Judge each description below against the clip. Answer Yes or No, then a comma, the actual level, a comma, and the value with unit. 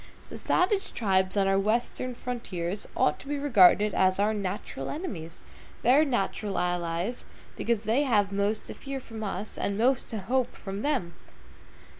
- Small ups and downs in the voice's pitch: No, average, 4.6 semitones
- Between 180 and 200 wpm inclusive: No, average, 160 wpm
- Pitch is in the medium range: No, high, 210 Hz